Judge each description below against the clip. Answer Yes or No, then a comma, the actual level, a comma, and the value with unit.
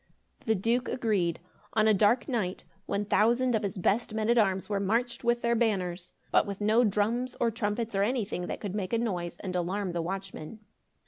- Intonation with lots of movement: No, average, 3.4 semitones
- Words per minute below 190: No, average, 200 wpm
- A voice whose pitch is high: Yes, high, 210 Hz